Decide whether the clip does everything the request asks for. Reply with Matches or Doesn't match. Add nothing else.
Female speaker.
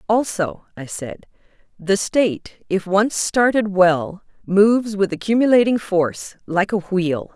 Matches